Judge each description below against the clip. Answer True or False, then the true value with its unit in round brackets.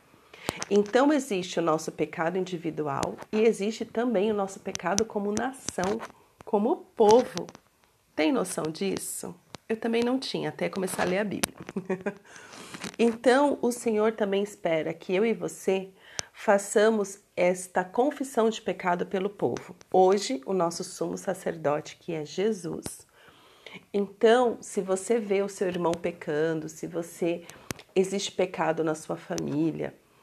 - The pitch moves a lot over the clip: False (4.1 semitones)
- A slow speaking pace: False (135 wpm)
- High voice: True (195 Hz)